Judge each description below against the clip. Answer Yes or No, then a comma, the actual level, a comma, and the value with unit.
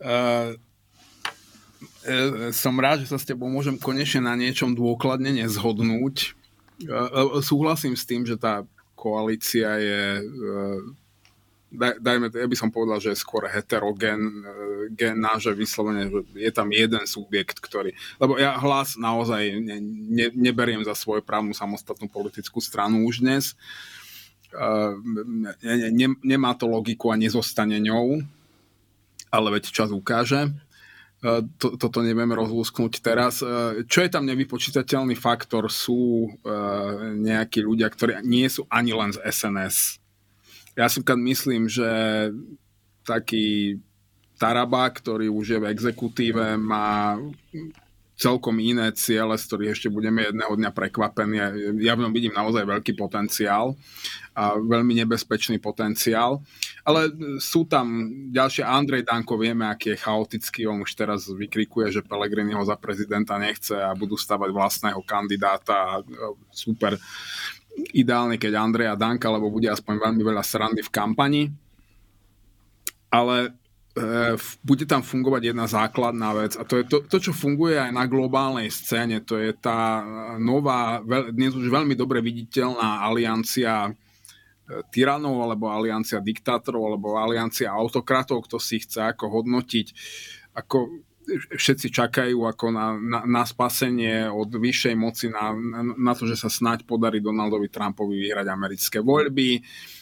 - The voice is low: Yes, low, 115 Hz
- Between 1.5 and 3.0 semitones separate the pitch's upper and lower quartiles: Yes, narrow, 2.6 semitones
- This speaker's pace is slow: No, average, 135 wpm